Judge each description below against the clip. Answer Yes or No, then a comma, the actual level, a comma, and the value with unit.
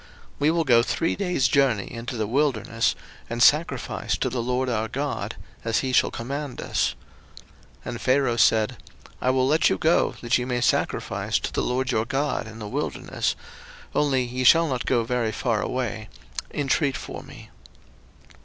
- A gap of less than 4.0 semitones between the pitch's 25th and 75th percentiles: Yes, average, 3.1 semitones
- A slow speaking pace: No, average, 175 wpm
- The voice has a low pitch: Yes, low, 125 Hz